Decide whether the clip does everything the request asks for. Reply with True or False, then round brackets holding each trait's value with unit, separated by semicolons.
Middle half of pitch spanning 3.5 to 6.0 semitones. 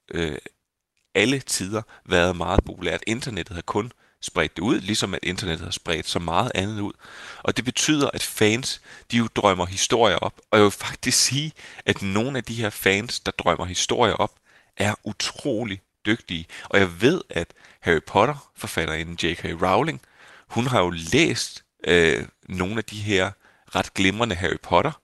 True (4.1 semitones)